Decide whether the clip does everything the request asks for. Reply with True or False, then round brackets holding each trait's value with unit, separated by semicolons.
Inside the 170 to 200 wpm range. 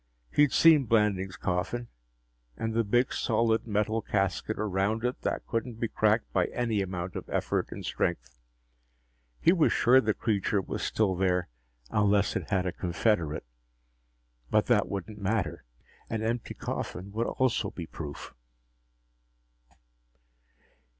False (135 wpm)